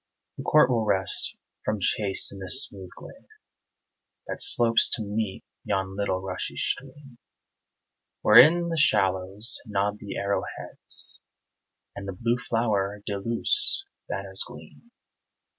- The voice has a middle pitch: No, low, 105 Hz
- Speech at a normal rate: No, slow, 130 wpm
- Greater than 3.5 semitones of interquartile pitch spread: Yes, average, 4.0 semitones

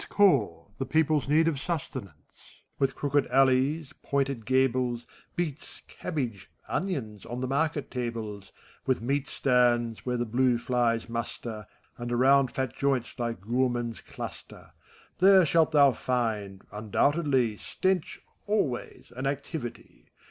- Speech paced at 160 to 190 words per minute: No, slow, 135 wpm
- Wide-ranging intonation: No, average, 3.2 semitones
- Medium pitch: No, low, 130 Hz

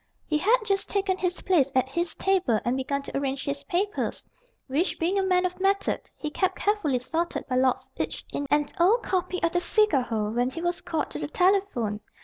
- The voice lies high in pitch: Yes, very high, 340 Hz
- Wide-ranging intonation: Yes, wide, 6.0 semitones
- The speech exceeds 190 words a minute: Yes, fast, 205 wpm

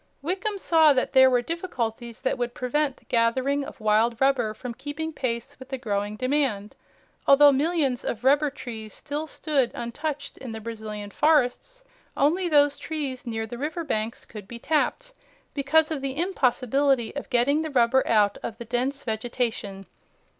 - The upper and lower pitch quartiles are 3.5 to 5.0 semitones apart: Yes, average, 4.2 semitones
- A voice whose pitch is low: No, very high, 260 Hz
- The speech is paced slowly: No, average, 165 wpm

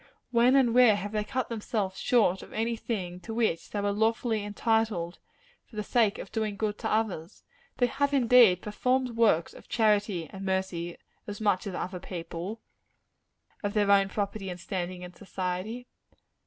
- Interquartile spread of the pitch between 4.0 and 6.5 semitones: No, average, 3.3 semitones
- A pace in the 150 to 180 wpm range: Yes, average, 170 wpm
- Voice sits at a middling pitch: No, high, 210 Hz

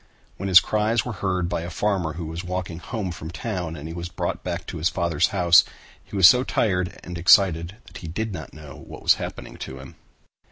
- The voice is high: No, very low, 90 Hz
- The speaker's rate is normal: No, fast, 220 wpm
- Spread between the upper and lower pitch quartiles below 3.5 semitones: Yes, average, 2.9 semitones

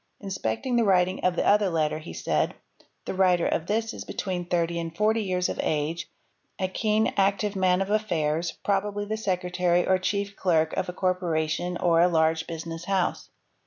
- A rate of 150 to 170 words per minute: No, average, 190 wpm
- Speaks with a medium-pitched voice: Yes, medium, 180 Hz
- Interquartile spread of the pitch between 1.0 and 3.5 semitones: Yes, average, 3.0 semitones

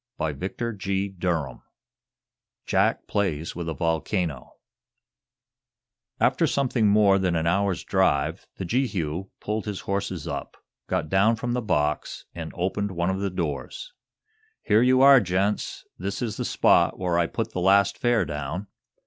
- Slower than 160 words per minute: Yes, average, 150 wpm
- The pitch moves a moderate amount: Yes, average, 3.7 semitones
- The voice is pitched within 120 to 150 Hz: No, very low, 95 Hz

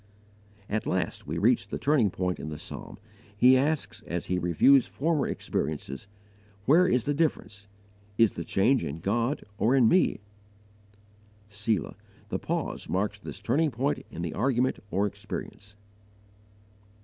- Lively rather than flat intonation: Yes, wide, 6.0 semitones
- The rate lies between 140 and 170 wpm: Yes, average, 145 wpm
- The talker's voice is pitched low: Yes, low, 110 Hz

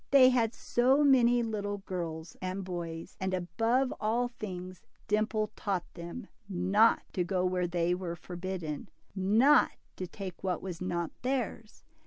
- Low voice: No, high, 190 Hz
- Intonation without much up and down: No, average, 4.3 semitones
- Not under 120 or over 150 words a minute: Yes, average, 145 wpm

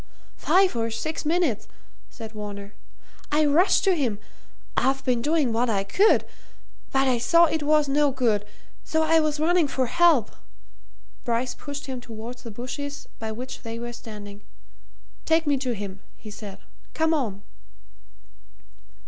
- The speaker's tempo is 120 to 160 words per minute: Yes, average, 155 wpm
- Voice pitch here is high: Yes, very high, 255 Hz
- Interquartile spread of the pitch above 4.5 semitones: Yes, wide, 5.4 semitones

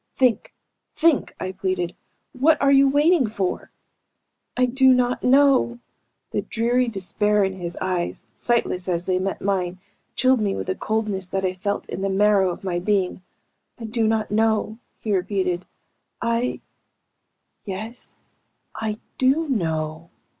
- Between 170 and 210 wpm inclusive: No, average, 145 wpm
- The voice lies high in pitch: Yes, high, 210 Hz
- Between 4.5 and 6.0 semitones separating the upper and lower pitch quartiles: Yes, average, 4.8 semitones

